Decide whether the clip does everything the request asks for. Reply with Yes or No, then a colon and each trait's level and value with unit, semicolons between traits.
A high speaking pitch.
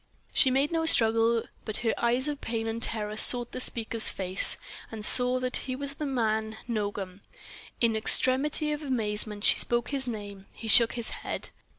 Yes: high, 230 Hz